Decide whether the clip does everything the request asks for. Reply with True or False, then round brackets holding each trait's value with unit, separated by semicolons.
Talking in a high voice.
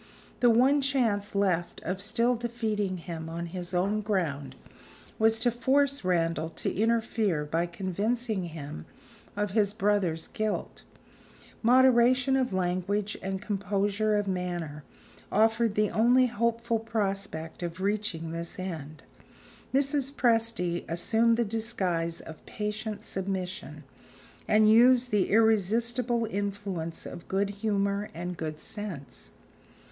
True (205 Hz)